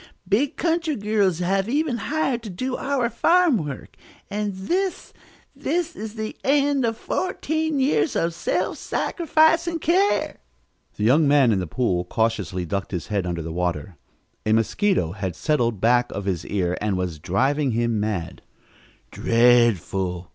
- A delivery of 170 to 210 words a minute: No, average, 155 wpm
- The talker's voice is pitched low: No, medium, 150 Hz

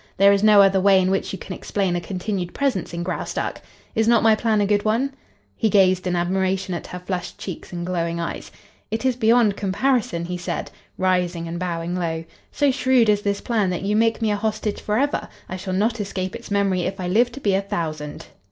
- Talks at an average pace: No, fast, 220 wpm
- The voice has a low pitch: No, high, 195 Hz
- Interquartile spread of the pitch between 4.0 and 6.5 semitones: No, average, 3.2 semitones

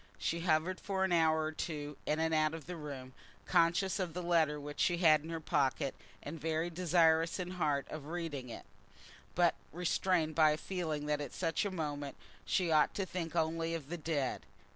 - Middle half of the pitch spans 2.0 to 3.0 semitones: Yes, narrow, 2.5 semitones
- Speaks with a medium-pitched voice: Yes, medium, 160 Hz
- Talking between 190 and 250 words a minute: Yes, average, 200 wpm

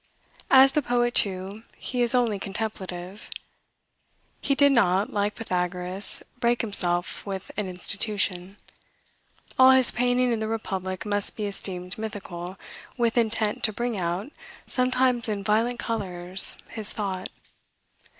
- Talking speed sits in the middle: No, slow, 130 wpm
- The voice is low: No, high, 210 Hz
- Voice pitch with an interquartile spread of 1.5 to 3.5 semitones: No, average, 4.2 semitones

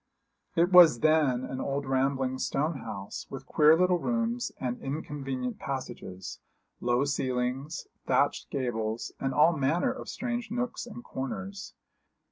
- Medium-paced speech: No, slow, 130 wpm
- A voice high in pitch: No, medium, 140 Hz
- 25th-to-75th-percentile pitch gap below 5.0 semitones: No, average, 5.3 semitones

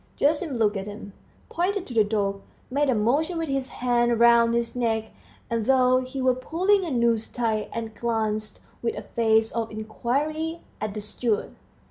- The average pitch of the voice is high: Yes, high, 235 Hz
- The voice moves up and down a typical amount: Yes, average, 3.4 semitones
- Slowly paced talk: No, average, 175 wpm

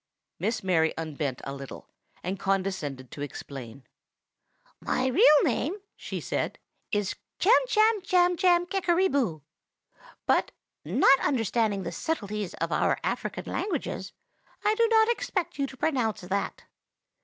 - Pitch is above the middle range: Yes, high, 225 Hz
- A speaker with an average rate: No, slow, 115 wpm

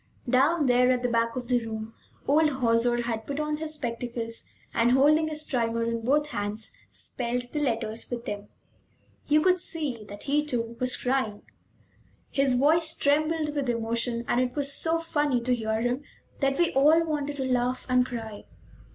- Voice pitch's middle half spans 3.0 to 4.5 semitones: Yes, average, 4.2 semitones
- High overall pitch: Yes, very high, 250 Hz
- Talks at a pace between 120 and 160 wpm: No, average, 175 wpm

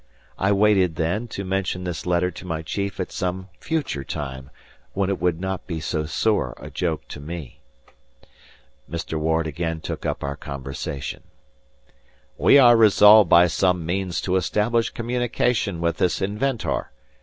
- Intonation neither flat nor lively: Yes, average, 4.0 semitones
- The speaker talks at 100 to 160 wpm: Yes, average, 155 wpm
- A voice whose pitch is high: No, very low, 90 Hz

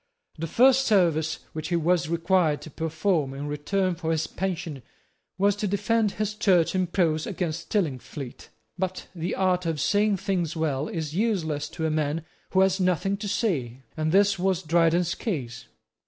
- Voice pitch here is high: No, medium, 170 Hz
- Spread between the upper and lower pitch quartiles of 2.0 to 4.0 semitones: Yes, average, 3.6 semitones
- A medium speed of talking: Yes, average, 170 wpm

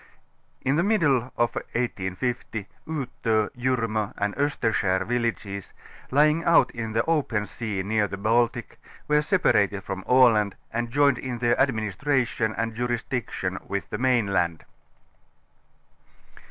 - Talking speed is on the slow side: Yes, slow, 120 wpm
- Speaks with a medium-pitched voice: No, low, 115 Hz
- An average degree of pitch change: Yes, average, 3.9 semitones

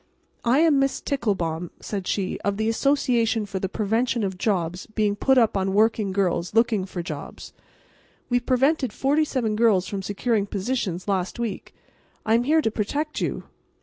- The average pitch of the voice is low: No, high, 215 Hz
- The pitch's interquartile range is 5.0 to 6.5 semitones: No, average, 4.2 semitones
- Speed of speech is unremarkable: Yes, average, 170 wpm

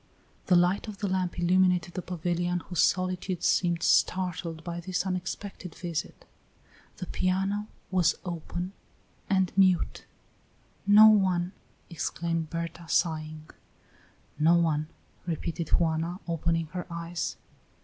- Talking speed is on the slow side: Yes, slow, 115 wpm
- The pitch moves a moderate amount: No, narrow, 1.8 semitones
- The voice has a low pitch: No, medium, 175 Hz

